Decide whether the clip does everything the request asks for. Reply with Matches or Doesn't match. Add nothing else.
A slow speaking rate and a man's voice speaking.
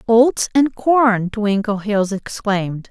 Doesn't match